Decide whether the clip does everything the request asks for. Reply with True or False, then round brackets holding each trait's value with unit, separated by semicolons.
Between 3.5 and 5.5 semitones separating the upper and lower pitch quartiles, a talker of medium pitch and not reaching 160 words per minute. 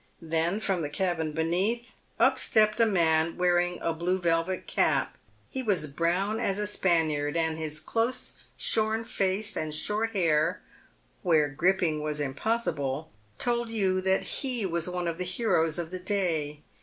False (4.6 semitones; 175 Hz; 165 wpm)